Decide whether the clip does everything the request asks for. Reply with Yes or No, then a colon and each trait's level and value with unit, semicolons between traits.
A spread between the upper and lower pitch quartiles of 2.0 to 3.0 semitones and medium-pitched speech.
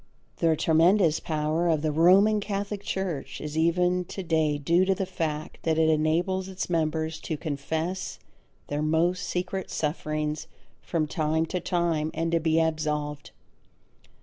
Yes: average, 2.7 semitones; medium, 160 Hz